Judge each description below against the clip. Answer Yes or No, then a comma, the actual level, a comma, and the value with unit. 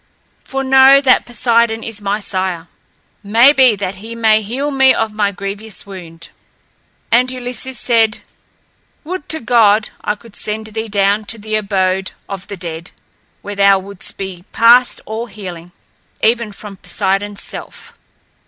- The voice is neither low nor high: No, high, 215 Hz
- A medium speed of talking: Yes, average, 150 wpm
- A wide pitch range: No, average, 3.0 semitones